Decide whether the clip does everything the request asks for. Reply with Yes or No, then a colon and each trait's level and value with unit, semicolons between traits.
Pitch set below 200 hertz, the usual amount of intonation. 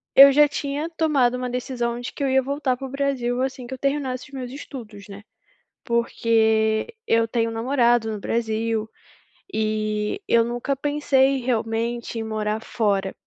No: high, 240 Hz; average, 3.3 semitones